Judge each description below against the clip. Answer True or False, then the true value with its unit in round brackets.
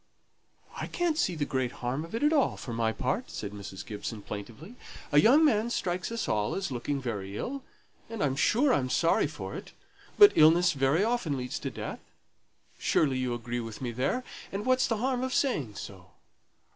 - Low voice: False (145 Hz)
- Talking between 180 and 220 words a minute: True (190 wpm)